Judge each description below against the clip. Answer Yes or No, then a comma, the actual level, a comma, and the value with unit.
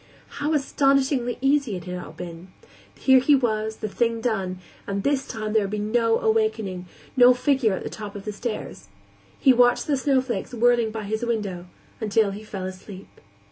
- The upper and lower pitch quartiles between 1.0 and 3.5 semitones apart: No, average, 4.4 semitones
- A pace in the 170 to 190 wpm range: Yes, average, 180 wpm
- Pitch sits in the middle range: No, high, 220 Hz